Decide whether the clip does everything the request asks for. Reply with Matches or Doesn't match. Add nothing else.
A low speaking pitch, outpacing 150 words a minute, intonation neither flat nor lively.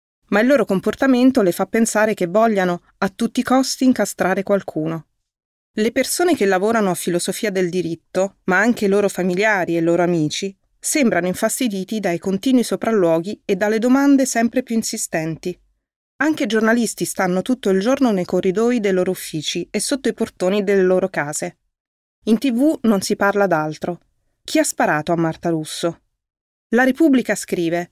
Doesn't match